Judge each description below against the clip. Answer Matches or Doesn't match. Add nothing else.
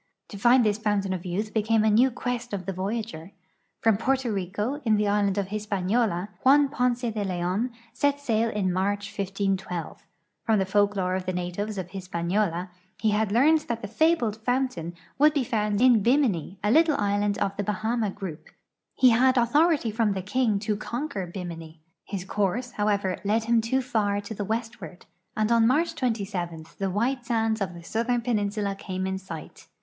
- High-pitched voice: Matches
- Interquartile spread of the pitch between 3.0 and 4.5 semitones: Matches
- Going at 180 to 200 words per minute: Matches